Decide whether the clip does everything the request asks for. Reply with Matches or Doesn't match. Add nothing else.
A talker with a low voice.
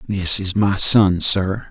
Matches